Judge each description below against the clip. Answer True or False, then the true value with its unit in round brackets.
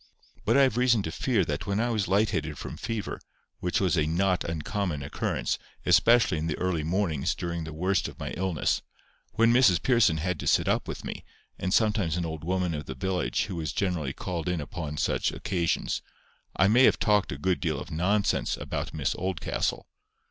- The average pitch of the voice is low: True (90 Hz)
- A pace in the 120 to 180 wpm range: False (195 wpm)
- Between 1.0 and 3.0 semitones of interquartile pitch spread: False (4.4 semitones)